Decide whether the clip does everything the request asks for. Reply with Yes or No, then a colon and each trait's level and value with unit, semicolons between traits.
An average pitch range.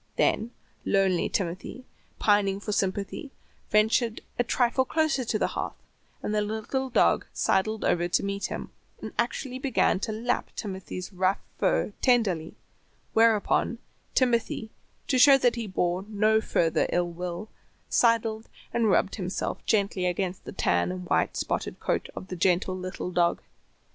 Yes: average, 3.9 semitones